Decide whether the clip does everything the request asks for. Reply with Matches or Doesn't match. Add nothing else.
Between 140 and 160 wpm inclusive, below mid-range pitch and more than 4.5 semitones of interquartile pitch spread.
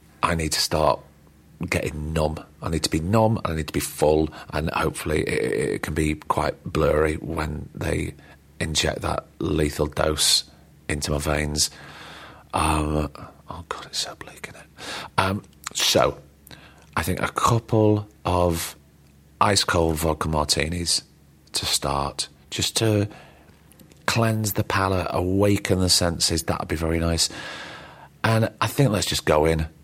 Doesn't match